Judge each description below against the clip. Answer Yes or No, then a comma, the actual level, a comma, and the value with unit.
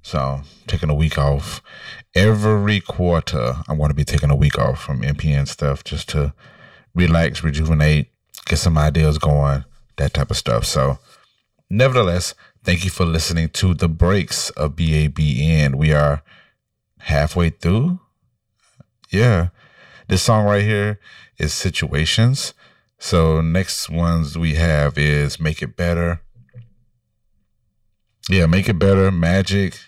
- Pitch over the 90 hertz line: No, very low, 85 Hz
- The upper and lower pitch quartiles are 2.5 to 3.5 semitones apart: No, average, 4.9 semitones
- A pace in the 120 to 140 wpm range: Yes, slow, 135 wpm